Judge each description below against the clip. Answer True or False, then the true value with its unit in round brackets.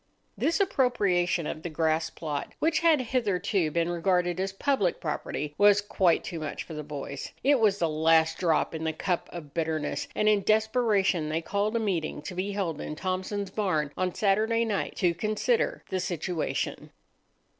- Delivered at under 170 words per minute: False (175 wpm)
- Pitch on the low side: False (185 Hz)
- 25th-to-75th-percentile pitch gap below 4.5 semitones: False (4.8 semitones)